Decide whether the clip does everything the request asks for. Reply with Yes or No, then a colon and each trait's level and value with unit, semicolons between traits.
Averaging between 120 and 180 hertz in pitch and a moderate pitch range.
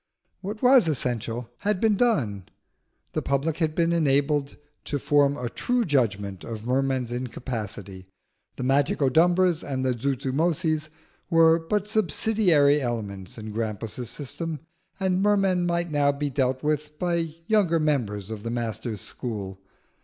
No: medium, 140 Hz; wide, 6.1 semitones